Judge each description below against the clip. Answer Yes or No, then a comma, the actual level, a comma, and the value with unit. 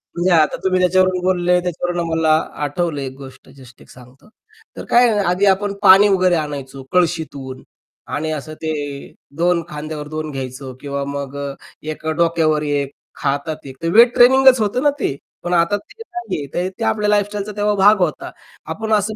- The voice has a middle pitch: Yes, medium, 170 Hz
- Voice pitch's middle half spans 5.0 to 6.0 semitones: Yes, wide, 5.4 semitones